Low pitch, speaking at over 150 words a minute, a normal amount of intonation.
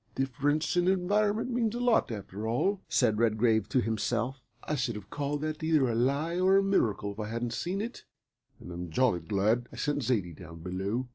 No: low, 125 Hz; average, 200 wpm; wide, 7.4 semitones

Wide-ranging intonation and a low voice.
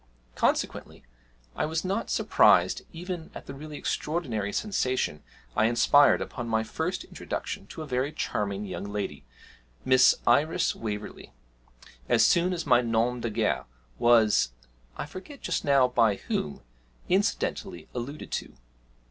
Yes: wide, 6.2 semitones; low, 125 Hz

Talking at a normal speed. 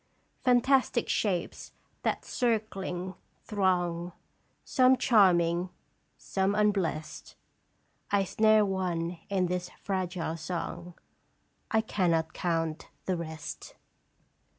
No: slow, 90 wpm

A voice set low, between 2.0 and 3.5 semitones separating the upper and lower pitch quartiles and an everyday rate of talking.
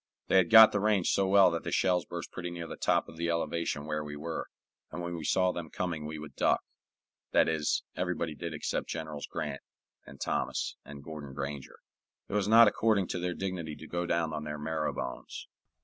No: very low, 85 Hz; average, 3.1 semitones; fast, 210 wpm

